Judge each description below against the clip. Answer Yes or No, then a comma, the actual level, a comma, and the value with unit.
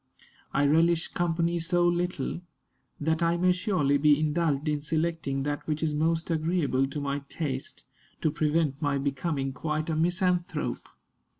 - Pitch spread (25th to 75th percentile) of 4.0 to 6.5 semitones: No, average, 2.8 semitones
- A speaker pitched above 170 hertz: No, medium, 155 Hz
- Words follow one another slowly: No, average, 145 wpm